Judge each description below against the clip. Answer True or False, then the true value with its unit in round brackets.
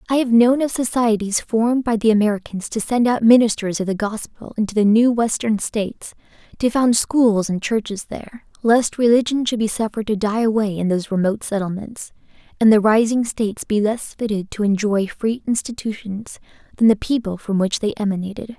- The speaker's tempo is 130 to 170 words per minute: False (185 wpm)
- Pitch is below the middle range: False (220 Hz)